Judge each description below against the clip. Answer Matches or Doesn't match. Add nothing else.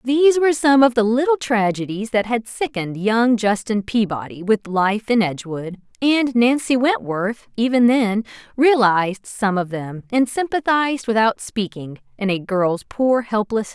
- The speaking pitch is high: Matches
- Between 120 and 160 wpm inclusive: Matches